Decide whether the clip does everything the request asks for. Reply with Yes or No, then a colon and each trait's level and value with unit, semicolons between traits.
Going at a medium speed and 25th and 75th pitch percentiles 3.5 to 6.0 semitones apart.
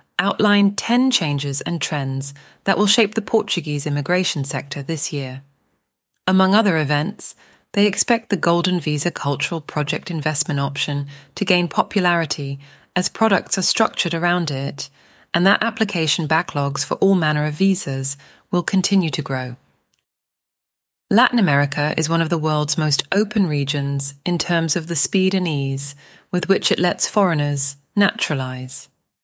Yes: average, 145 wpm; average, 5.0 semitones